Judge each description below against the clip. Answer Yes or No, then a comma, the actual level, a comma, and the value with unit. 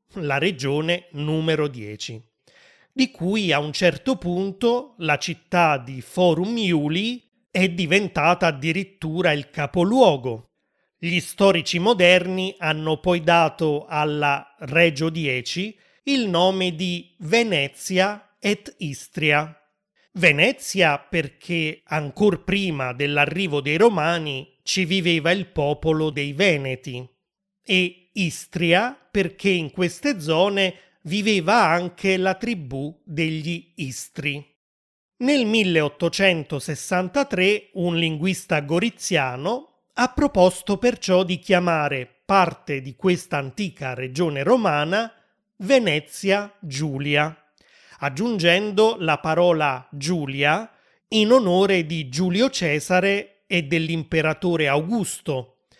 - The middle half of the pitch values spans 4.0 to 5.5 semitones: Yes, average, 4.4 semitones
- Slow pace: Yes, slow, 95 wpm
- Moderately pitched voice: Yes, medium, 175 Hz